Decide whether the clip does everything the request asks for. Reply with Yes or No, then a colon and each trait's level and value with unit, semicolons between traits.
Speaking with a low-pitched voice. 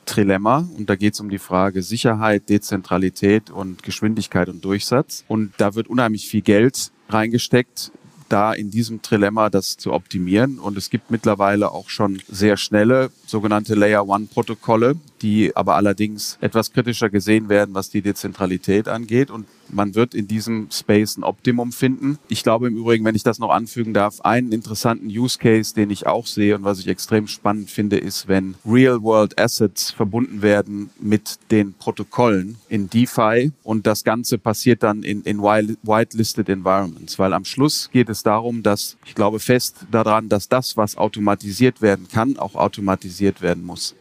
Yes: low, 110 Hz